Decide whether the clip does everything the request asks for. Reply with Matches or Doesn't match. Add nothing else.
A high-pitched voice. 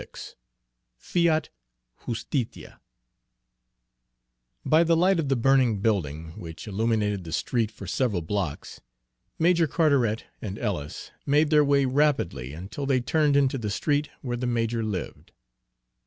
Doesn't match